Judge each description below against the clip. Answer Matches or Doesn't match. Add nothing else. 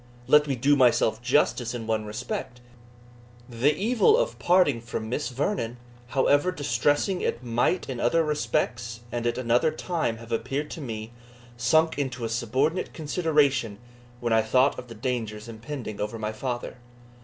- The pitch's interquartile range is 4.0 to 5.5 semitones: Matches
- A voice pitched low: Matches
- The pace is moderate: Matches